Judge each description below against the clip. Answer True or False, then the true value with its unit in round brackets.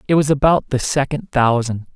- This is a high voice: False (140 Hz)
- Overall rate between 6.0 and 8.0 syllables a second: False (5.1 syllables/s)